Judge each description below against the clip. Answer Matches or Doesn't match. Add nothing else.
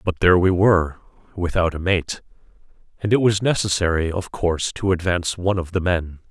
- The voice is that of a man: Matches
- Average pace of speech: Matches